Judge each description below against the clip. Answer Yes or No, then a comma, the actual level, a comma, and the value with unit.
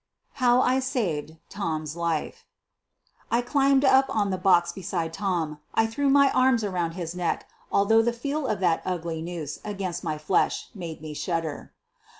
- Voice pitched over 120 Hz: Yes, medium, 185 Hz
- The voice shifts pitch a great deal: Yes, wide, 6.5 semitones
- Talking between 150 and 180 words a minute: Yes, average, 160 wpm